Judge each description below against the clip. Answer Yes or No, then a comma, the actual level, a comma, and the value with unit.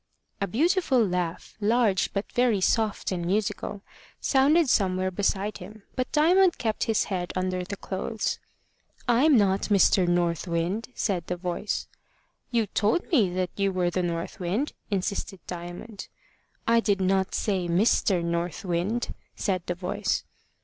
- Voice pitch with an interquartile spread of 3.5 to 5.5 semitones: Yes, average, 3.8 semitones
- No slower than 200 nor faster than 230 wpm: No, average, 145 wpm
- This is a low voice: No, high, 195 Hz